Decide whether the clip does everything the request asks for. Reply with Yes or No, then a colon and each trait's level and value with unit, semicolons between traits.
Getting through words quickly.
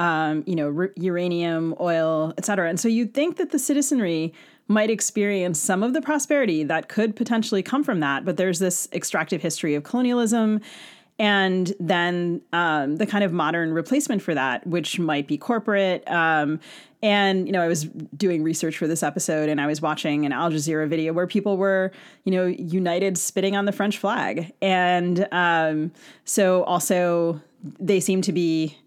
No: average, 180 wpm